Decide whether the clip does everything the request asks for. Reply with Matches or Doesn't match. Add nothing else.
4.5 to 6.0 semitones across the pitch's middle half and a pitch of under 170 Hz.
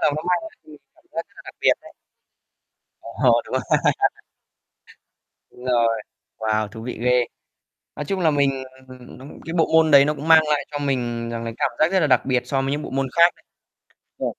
Doesn't match